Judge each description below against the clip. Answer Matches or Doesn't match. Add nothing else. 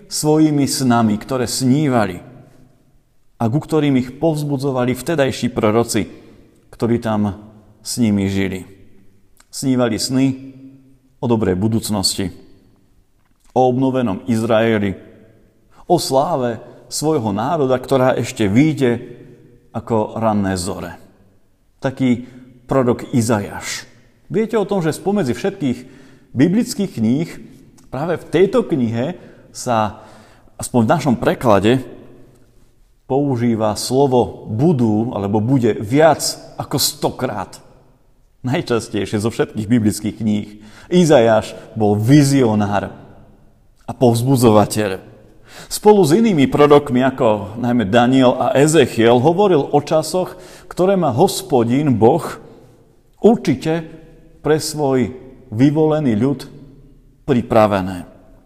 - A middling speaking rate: Doesn't match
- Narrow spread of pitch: Doesn't match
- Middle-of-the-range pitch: Doesn't match